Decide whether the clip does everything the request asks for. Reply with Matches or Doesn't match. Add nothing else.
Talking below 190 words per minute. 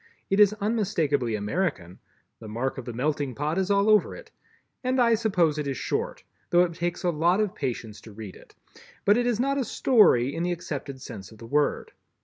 Doesn't match